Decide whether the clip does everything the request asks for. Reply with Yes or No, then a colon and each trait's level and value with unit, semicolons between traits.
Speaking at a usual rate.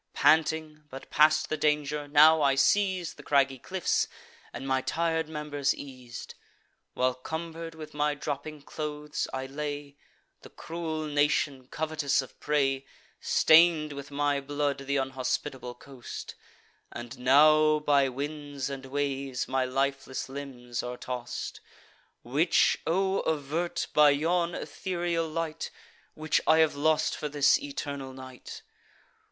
No: slow, 130 wpm